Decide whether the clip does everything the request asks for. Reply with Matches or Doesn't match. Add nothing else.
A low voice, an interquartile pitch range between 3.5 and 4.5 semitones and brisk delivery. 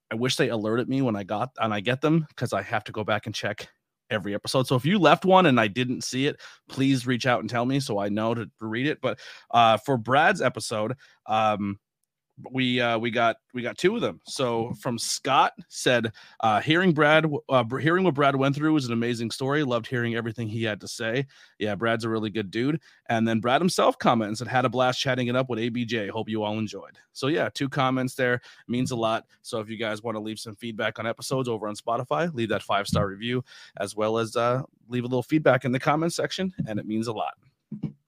Doesn't match